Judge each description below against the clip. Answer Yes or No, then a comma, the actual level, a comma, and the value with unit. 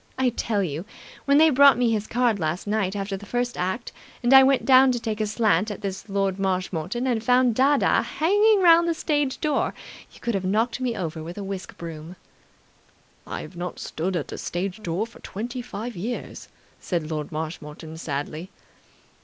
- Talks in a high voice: Yes, high, 210 Hz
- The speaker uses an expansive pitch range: Yes, wide, 5.7 semitones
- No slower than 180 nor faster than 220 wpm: Yes, average, 190 wpm